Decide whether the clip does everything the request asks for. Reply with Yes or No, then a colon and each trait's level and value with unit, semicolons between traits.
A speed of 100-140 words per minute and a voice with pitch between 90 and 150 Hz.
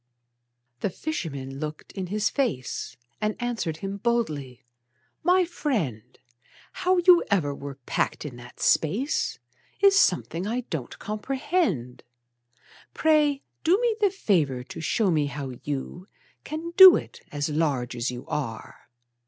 No: slow, 135 wpm; medium, 185 Hz